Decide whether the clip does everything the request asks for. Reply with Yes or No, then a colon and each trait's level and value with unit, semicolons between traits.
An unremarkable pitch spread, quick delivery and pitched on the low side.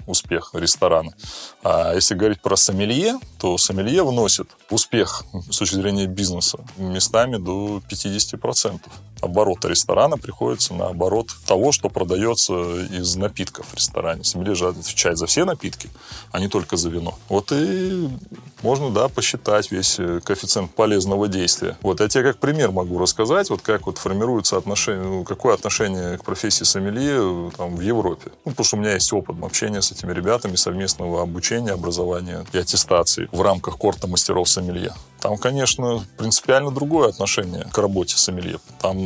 No: average, 3.2 semitones; average, 150 wpm; very low, 95 Hz